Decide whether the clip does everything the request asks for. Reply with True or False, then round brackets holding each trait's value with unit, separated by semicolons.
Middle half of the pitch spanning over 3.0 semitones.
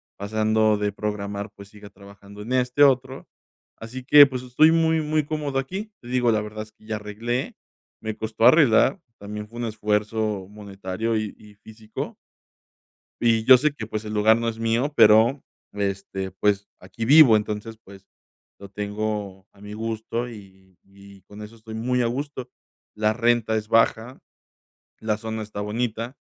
False (2.7 semitones)